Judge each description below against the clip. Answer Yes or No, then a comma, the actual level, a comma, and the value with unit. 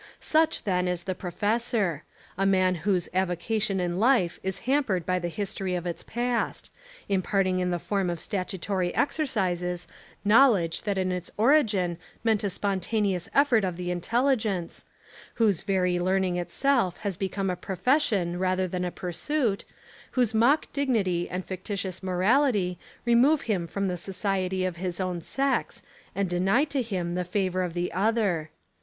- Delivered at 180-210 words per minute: No, average, 160 wpm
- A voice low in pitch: No, high, 190 Hz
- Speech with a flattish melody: No, average, 3.6 semitones